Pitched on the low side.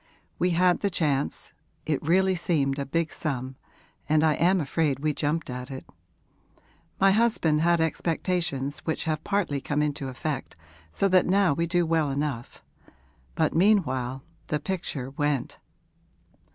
No: medium, 155 Hz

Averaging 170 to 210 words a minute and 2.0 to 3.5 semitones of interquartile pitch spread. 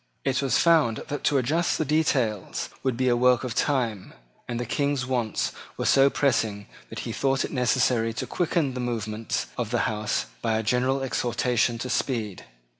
Yes: average, 185 wpm; average, 3.0 semitones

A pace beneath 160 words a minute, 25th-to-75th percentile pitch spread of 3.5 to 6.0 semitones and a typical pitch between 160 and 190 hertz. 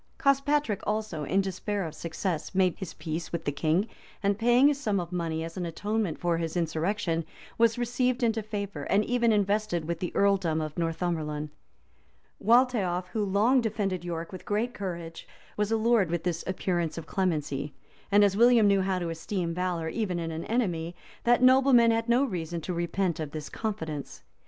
No: average, 180 wpm; average, 4.8 semitones; medium, 185 Hz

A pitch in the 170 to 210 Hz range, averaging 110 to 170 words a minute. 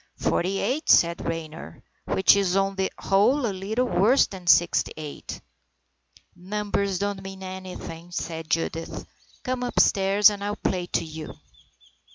Yes: high, 190 Hz; average, 150 wpm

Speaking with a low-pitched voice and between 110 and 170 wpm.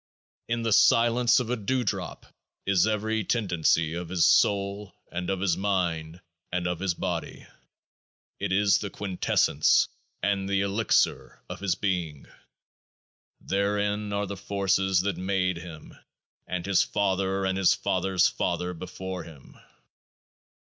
Yes: very low, 95 Hz; slow, 135 wpm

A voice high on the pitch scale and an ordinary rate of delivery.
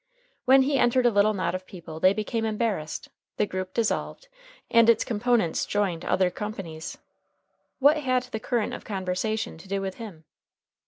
Yes: high, 210 Hz; average, 170 wpm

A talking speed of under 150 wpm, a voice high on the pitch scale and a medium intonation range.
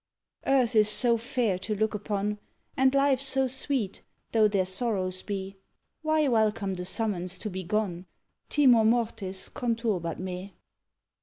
Yes: average, 140 wpm; high, 215 Hz; average, 4.3 semitones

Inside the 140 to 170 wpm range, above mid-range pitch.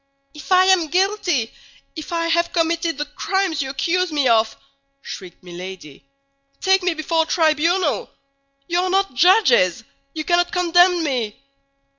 Yes: average, 145 wpm; very high, 330 Hz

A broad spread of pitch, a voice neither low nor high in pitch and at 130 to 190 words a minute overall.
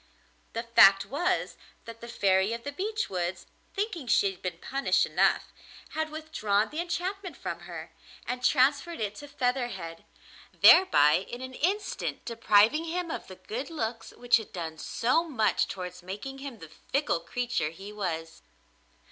No: wide, 7.9 semitones; high, 235 Hz; average, 155 wpm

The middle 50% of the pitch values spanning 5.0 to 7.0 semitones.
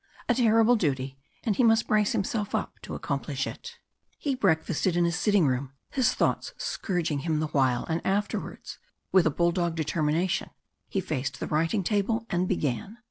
Yes: wide, 5.6 semitones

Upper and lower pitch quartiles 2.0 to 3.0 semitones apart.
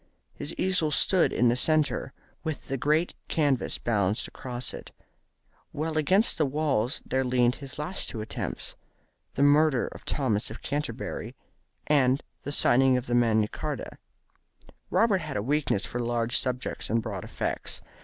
No: average, 4.1 semitones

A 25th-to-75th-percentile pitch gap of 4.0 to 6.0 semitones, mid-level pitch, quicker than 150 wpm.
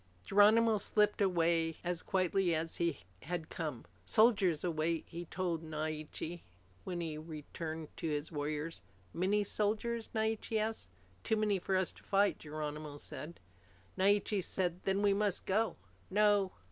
No: average, 4.4 semitones; medium, 180 Hz; average, 145 wpm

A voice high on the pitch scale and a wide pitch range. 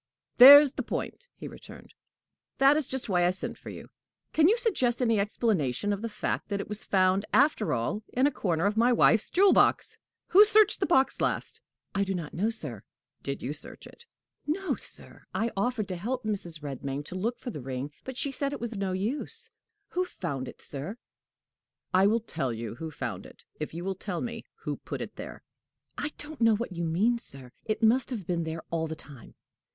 Yes: high, 205 Hz; wide, 7.4 semitones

